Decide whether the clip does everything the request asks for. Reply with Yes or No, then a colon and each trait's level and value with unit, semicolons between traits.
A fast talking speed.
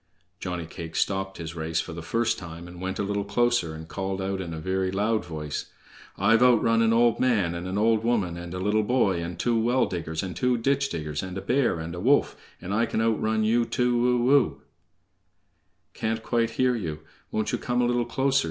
Yes: fast, 215 wpm